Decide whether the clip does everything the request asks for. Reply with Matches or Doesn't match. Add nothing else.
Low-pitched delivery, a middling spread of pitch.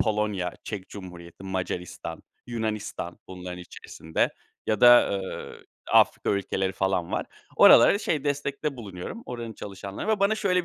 Matches